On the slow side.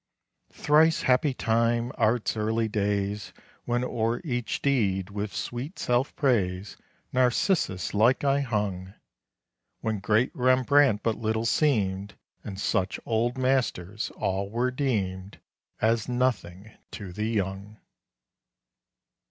Yes: slow, 110 wpm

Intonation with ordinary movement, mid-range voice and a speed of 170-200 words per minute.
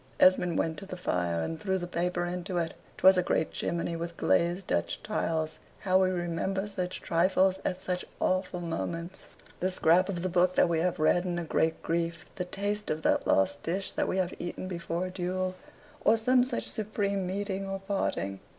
No: narrow, 2.1 semitones; medium, 180 Hz; average, 195 wpm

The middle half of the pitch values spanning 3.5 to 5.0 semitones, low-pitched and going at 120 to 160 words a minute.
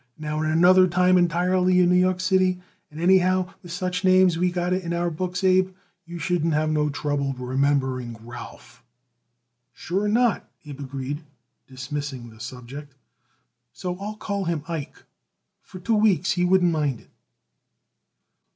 No: average, 4.1 semitones; medium, 175 Hz; average, 155 wpm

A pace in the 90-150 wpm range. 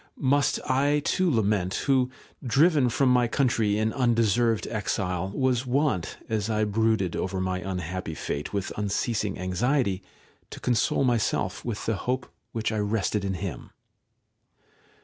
Yes: average, 140 wpm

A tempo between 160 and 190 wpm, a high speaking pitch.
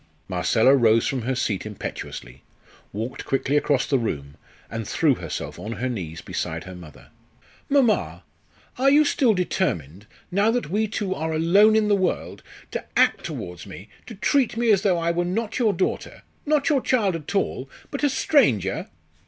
No: average, 175 wpm; medium, 160 Hz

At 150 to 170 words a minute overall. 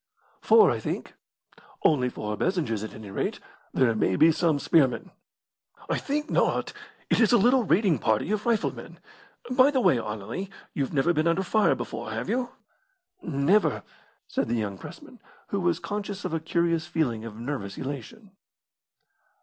Yes: average, 165 wpm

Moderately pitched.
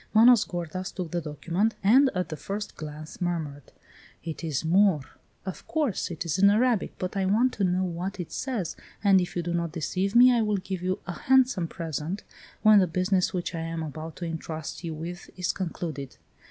Yes: medium, 180 Hz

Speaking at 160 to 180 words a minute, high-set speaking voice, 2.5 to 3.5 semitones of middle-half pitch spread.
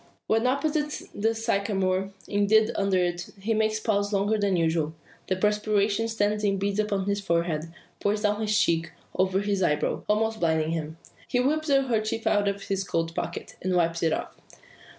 Yes: average, 175 wpm; high, 200 Hz; average, 2.9 semitones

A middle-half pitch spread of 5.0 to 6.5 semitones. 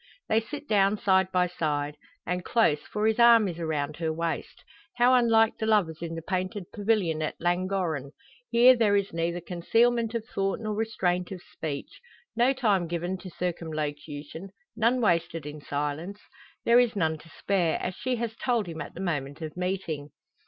Yes: average, 5.3 semitones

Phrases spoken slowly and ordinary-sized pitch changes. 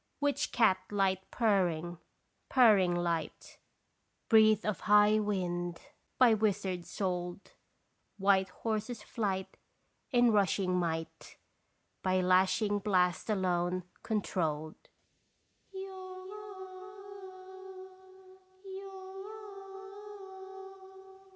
Yes: slow, 65 wpm; average, 3.0 semitones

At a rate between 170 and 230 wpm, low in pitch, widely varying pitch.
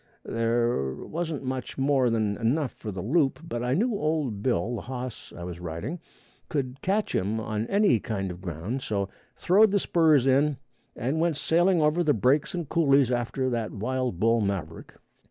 Yes: average, 175 wpm; low, 125 Hz; wide, 5.9 semitones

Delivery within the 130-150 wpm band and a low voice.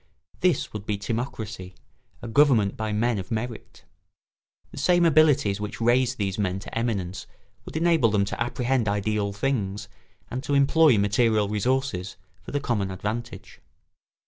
Yes: average, 145 wpm; low, 110 Hz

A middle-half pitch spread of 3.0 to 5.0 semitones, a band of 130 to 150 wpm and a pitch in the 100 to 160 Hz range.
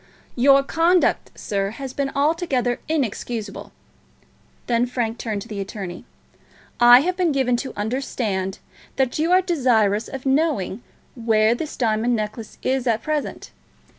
No: average, 4.3 semitones; slow, 135 wpm; high, 245 Hz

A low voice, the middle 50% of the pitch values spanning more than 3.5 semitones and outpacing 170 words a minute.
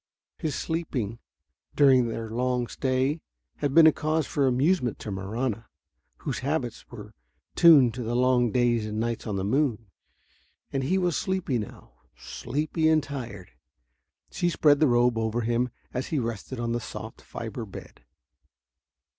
No: low, 125 Hz; average, 4.2 semitones; average, 155 wpm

